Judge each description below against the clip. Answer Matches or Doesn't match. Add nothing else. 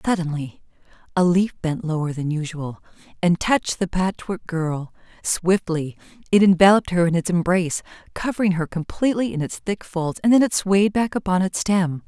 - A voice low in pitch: Doesn't match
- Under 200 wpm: Matches